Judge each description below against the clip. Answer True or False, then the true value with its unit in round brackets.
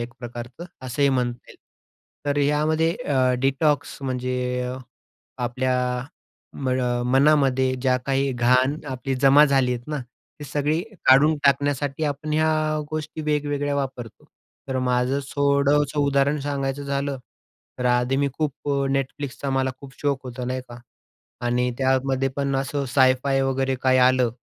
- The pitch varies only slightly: True (2.0 semitones)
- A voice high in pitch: False (135 Hz)